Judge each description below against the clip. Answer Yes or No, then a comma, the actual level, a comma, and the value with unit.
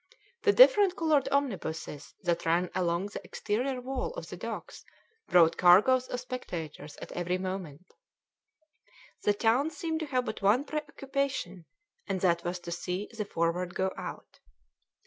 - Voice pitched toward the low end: No, high, 200 Hz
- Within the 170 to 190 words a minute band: No, average, 150 wpm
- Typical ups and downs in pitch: No, wide, 7.4 semitones